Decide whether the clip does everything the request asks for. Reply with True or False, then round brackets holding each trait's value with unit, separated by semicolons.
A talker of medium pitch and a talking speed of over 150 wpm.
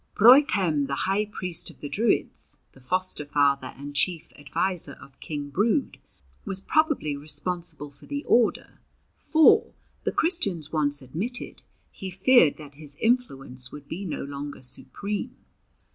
False (165 Hz; 140 wpm)